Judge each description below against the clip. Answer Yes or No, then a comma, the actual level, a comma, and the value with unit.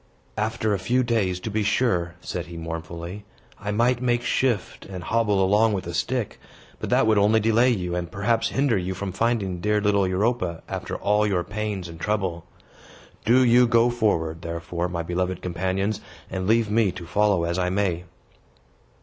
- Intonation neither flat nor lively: Yes, average, 3.9 semitones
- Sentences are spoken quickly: No, average, 180 wpm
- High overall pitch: No, low, 100 Hz